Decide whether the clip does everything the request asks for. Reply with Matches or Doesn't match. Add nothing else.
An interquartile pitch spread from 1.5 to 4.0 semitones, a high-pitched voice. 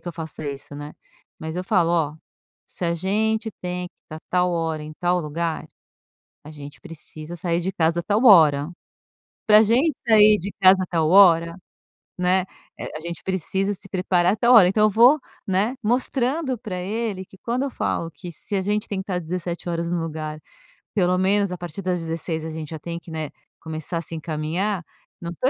Doesn't match